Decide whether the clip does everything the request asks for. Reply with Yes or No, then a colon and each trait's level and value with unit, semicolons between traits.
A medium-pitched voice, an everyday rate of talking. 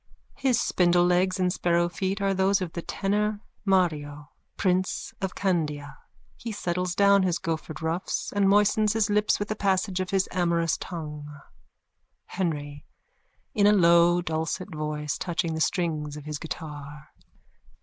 Yes: medium, 175 Hz; average, 145 wpm